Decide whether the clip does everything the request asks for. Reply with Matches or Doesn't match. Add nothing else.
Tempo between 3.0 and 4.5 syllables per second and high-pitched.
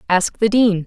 Matches